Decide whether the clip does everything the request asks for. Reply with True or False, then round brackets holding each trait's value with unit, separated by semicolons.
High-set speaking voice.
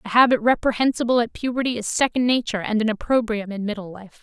True (230 Hz)